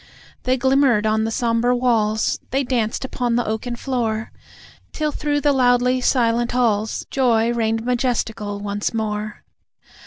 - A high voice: Yes, high, 235 Hz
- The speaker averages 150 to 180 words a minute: No, slow, 135 wpm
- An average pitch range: No, narrow, 2.3 semitones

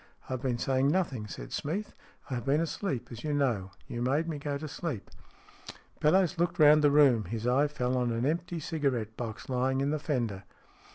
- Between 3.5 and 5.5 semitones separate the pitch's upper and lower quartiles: Yes, average, 4.0 semitones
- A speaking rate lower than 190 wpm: No, average, 195 wpm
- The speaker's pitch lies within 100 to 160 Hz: Yes, low, 135 Hz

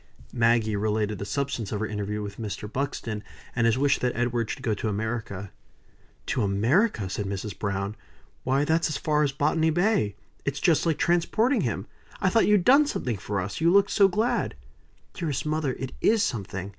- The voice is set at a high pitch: No, low, 120 Hz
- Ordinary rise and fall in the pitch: No, wide, 7.3 semitones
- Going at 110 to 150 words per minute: No, average, 185 wpm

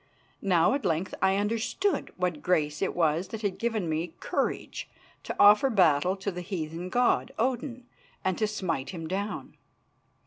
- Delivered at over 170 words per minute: No, average, 160 wpm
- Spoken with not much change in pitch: No, average, 4.3 semitones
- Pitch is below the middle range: No, high, 190 Hz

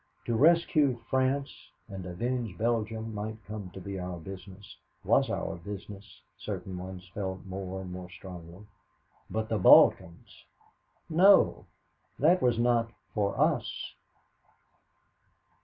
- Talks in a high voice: No, low, 105 Hz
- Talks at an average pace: No, slow, 120 wpm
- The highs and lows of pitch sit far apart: No, average, 4.1 semitones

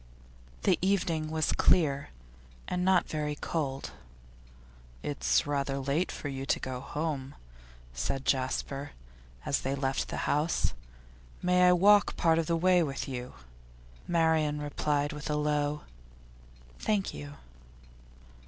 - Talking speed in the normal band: No, slow, 125 wpm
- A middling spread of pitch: Yes, average, 3.3 semitones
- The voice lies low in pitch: No, medium, 150 Hz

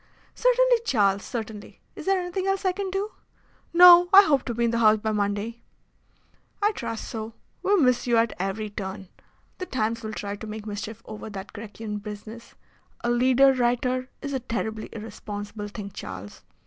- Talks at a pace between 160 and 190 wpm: Yes, average, 180 wpm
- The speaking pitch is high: Yes, high, 230 Hz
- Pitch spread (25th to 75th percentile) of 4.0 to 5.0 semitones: Yes, average, 4.6 semitones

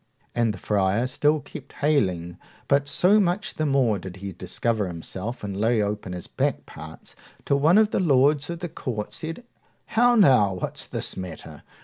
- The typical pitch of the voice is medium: No, low, 120 Hz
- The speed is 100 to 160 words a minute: No, average, 175 wpm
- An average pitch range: No, wide, 8.1 semitones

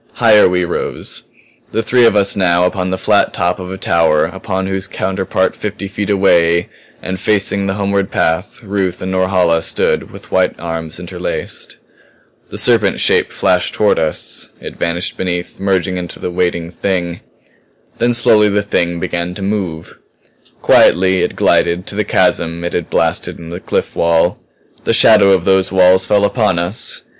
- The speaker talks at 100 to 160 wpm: No, average, 170 wpm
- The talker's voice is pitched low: Yes, very low, 95 Hz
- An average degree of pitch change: No, narrow, 2.3 semitones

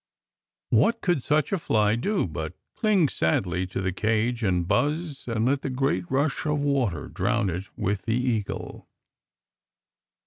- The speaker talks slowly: No, average, 150 wpm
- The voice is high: No, low, 120 Hz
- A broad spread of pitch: Yes, wide, 7.1 semitones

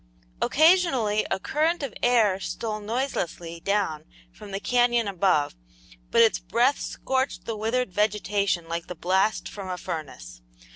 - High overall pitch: Yes, high, 210 Hz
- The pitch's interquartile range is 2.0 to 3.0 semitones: No, average, 4.9 semitones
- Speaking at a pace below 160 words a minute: Yes, average, 140 wpm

